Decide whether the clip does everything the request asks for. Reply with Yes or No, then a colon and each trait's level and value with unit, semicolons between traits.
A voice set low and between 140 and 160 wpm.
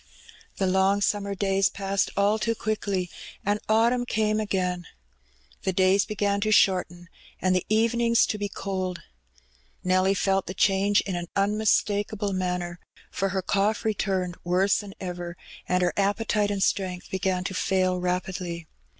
No: high, 195 Hz; average, 150 wpm